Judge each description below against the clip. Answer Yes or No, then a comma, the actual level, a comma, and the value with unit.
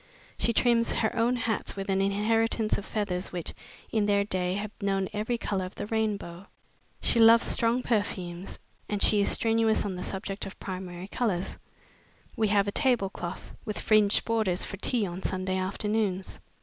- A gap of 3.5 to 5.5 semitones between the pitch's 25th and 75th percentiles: No, average, 2.8 semitones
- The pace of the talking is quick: No, average, 175 wpm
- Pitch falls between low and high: No, high, 205 Hz